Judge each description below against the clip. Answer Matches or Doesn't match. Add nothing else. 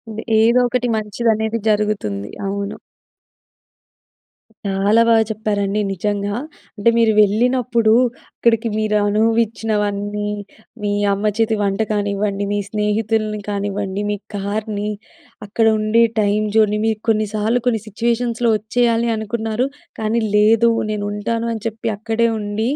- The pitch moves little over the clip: Matches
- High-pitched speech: Matches